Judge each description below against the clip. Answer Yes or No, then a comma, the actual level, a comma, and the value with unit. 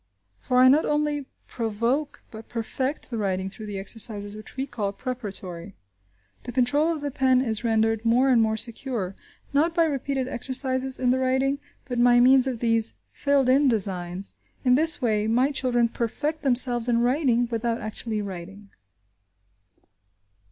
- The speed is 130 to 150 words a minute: No, average, 160 wpm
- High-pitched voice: Yes, high, 245 Hz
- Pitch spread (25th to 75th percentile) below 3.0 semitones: No, average, 3.4 semitones